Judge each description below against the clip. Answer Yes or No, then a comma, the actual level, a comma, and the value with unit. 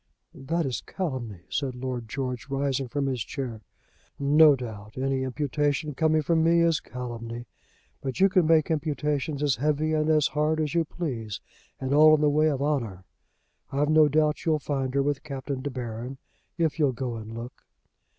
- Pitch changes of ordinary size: Yes, average, 3.3 semitones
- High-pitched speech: No, medium, 140 Hz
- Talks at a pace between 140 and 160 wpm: No, average, 180 wpm